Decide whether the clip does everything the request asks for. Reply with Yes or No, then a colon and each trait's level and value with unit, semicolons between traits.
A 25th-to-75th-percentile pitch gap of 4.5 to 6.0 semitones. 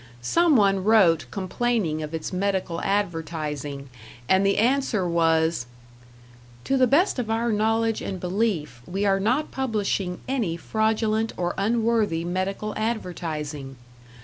Yes: average, 5.1 semitones